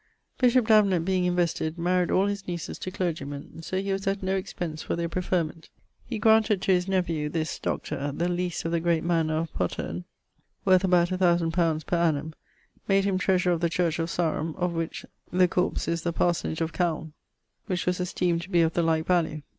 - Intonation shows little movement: Yes, narrow, 2.2 semitones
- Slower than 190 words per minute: No, fast, 205 wpm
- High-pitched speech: No, medium, 175 Hz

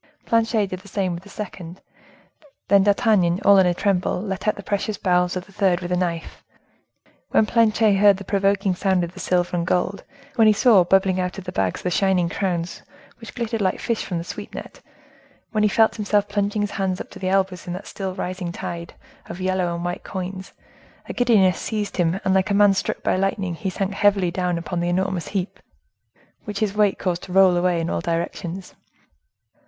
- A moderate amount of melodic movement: No, narrow, 2.2 semitones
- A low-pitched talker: No, high, 190 Hz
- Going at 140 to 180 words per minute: No, fast, 205 wpm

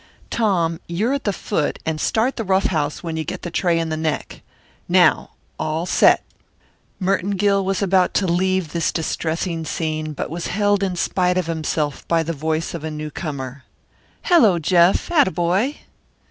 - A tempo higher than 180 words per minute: No, average, 175 wpm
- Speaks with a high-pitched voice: No, medium, 170 Hz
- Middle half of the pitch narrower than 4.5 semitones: Yes, average, 3.4 semitones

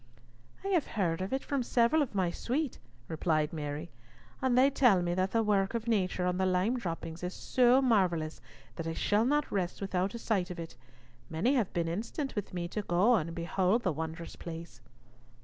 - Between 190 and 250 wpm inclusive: Yes, average, 200 wpm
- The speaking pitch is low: No, high, 190 Hz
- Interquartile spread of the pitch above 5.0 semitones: Yes, wide, 5.6 semitones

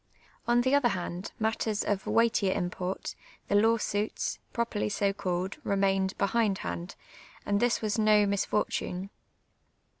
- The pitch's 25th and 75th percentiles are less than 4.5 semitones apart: Yes, narrow, 2.6 semitones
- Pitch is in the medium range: No, high, 205 Hz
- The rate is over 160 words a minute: No, average, 140 wpm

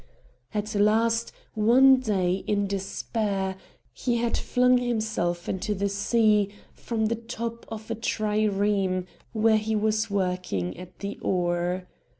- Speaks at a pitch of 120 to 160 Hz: No, high, 210 Hz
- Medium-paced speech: No, slow, 130 wpm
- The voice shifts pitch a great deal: No, average, 2.9 semitones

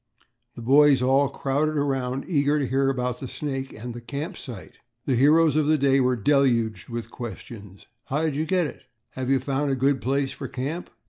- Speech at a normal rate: Yes, average, 195 wpm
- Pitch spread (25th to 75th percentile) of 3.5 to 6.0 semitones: No, narrow, 2.5 semitones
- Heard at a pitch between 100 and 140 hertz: Yes, low, 135 Hz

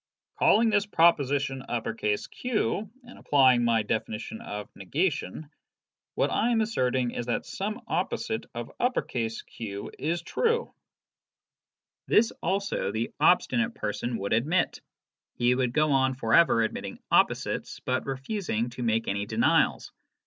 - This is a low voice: Yes, low, 130 Hz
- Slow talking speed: Yes, slow, 130 wpm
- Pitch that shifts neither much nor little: No, wide, 8.5 semitones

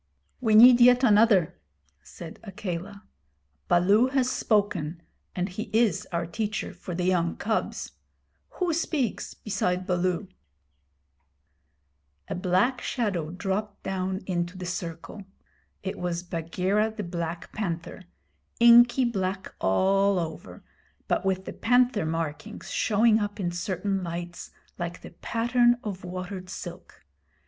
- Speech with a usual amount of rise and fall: Yes, average, 3.8 semitones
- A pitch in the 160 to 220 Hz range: Yes, high, 190 Hz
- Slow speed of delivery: Yes, slow, 120 wpm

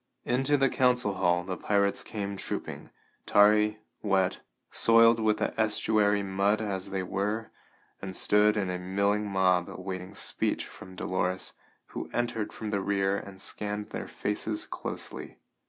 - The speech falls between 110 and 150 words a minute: Yes, average, 145 wpm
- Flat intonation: Yes, narrow, 2.0 semitones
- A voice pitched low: Yes, low, 100 Hz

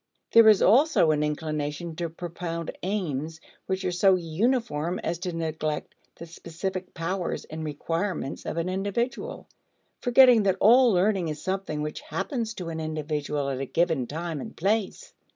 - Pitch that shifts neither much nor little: Yes, average, 4.2 semitones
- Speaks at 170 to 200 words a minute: No, average, 155 wpm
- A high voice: No, medium, 175 Hz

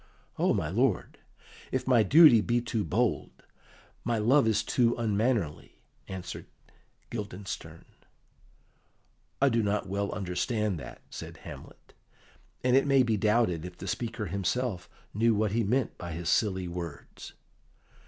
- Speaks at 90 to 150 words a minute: Yes, slow, 135 wpm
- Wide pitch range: No, average, 4.2 semitones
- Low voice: Yes, low, 105 Hz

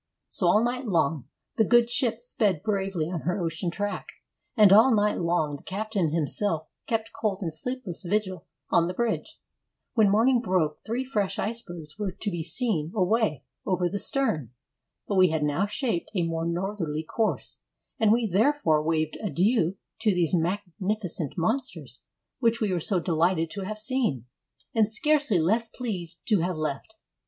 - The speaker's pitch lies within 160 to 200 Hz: Yes, high, 190 Hz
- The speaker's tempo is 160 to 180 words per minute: Yes, average, 165 wpm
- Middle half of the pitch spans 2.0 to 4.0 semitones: No, average, 4.9 semitones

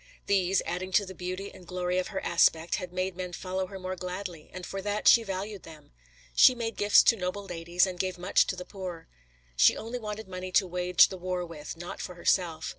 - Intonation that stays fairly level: Yes, narrow, 1.7 semitones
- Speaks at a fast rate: Yes, fast, 220 wpm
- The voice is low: No, medium, 185 Hz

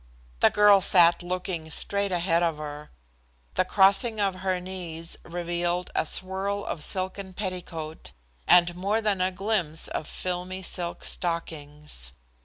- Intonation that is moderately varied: No, narrow, 2.3 semitones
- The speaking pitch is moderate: Yes, medium, 180 Hz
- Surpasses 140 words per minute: No, slow, 135 wpm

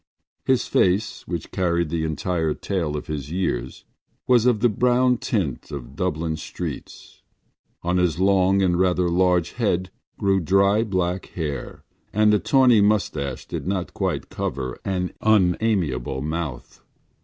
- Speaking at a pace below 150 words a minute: Yes, average, 140 wpm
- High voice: No, very low, 90 Hz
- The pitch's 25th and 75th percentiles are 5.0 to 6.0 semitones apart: No, average, 4.1 semitones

